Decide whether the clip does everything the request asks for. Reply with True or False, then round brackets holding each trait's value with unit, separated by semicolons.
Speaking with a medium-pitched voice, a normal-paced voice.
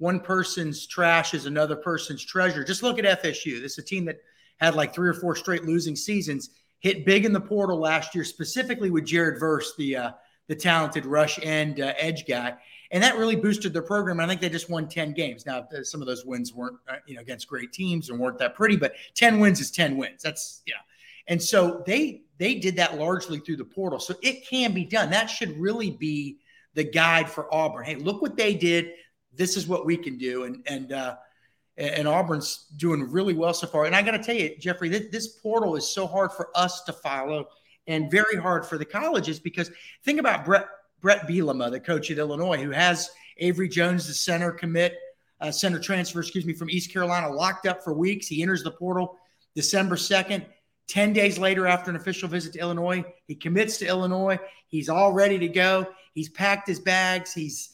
False (175 Hz; 215 wpm)